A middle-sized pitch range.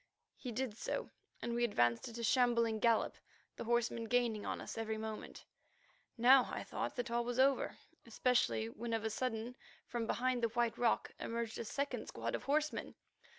No: narrow, 1.7 semitones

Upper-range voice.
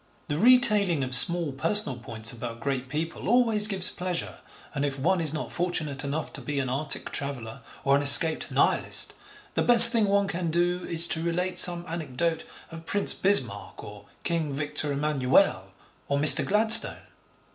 No: medium, 160 Hz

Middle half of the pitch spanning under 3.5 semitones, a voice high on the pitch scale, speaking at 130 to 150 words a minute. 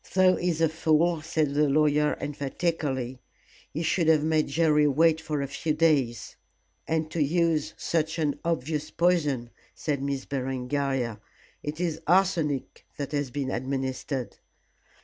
No: average, 2.7 semitones; medium, 150 Hz; average, 140 wpm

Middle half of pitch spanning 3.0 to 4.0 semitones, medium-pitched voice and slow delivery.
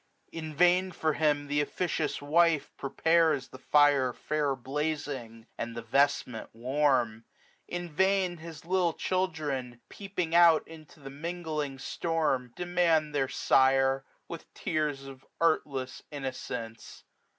Yes: average, 3.7 semitones; medium, 150 Hz; slow, 125 wpm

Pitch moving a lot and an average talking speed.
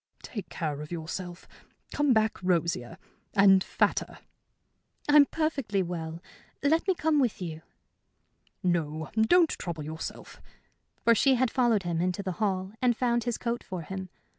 Yes: wide, 6.2 semitones; average, 145 wpm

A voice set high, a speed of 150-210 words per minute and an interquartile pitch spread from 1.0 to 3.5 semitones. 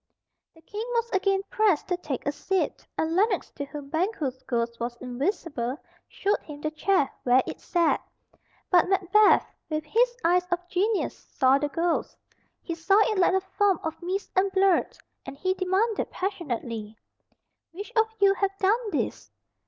No: very high, 360 Hz; average, 165 wpm; average, 5.2 semitones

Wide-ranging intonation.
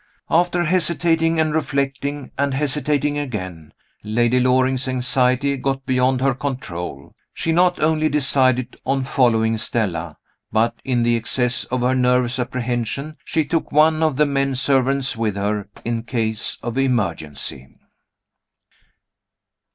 No: average, 3.3 semitones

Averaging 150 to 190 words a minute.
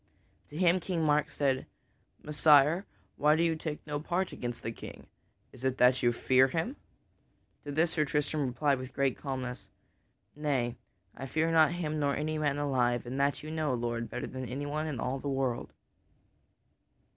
Yes: average, 180 wpm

